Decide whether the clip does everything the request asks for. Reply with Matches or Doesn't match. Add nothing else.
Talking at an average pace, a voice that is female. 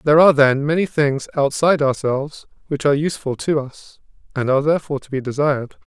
Doesn't match